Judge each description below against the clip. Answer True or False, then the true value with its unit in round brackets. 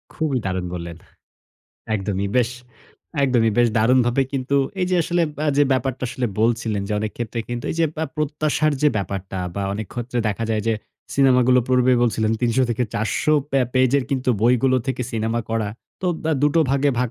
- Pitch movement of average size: True (3.3 semitones)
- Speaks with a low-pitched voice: True (120 Hz)